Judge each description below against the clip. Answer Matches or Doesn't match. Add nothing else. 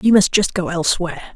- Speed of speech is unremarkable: Doesn't match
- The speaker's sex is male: Doesn't match